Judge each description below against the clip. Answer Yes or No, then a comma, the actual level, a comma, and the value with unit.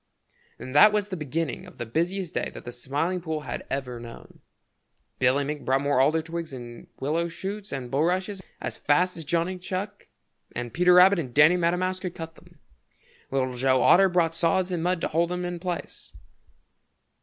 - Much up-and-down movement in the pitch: No, average, 4.7 semitones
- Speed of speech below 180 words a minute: No, average, 190 wpm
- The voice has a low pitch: No, medium, 165 Hz